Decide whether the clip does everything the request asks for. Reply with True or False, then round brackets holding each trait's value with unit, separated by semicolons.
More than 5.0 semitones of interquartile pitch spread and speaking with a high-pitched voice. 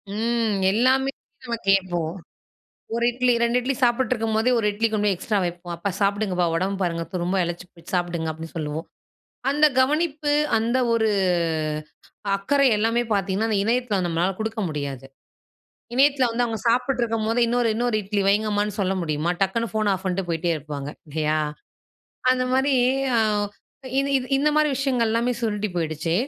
True (5.4 semitones; 215 Hz)